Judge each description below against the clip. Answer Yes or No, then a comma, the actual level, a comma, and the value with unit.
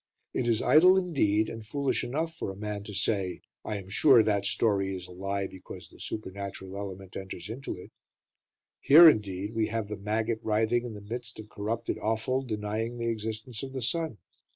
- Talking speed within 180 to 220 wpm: Yes, average, 190 wpm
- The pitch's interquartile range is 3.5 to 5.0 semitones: No, average, 3.1 semitones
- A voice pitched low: Yes, low, 110 Hz